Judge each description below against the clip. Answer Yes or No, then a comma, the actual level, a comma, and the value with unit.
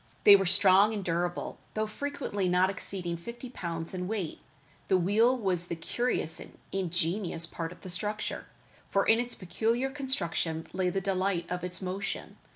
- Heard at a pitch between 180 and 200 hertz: Yes, high, 190 Hz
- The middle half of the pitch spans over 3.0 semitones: Yes, average, 3.5 semitones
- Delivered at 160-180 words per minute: Yes, average, 165 wpm